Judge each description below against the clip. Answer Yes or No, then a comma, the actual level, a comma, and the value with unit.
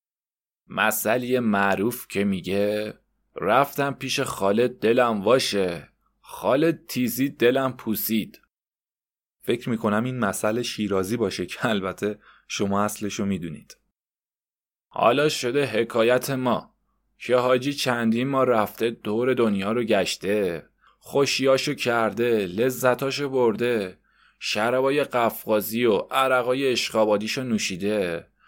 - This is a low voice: Yes, low, 120 Hz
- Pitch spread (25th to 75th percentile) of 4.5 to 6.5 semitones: No, average, 3.7 semitones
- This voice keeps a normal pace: No, slow, 100 wpm